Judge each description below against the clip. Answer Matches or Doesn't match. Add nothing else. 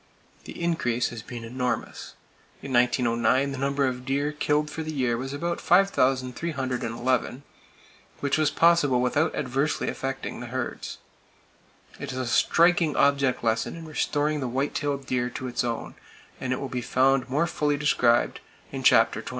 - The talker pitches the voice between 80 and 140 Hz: Matches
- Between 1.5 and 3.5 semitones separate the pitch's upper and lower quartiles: Matches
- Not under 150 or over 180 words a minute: Matches